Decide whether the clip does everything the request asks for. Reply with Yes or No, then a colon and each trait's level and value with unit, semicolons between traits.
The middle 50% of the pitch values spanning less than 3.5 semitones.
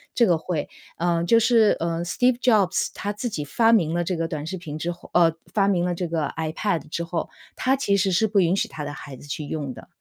No: average, 4.0 semitones